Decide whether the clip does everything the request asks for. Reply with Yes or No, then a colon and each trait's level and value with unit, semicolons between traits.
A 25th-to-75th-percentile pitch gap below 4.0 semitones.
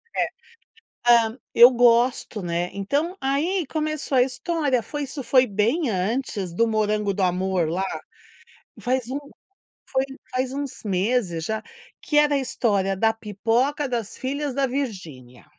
No: wide, 5.4 semitones